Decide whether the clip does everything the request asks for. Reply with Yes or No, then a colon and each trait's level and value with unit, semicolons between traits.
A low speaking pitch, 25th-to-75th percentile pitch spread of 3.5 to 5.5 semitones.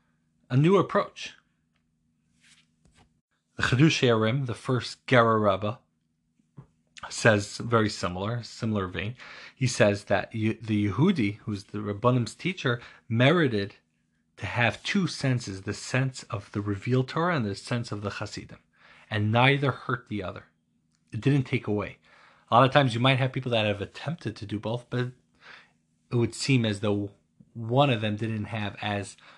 Yes: low, 110 Hz; average, 3.9 semitones